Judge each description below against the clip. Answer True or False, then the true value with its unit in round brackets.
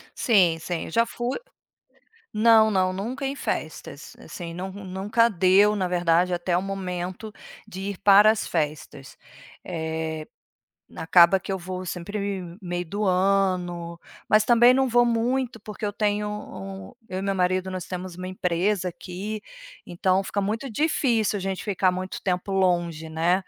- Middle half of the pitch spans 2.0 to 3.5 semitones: True (2.9 semitones)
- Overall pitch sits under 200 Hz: True (190 Hz)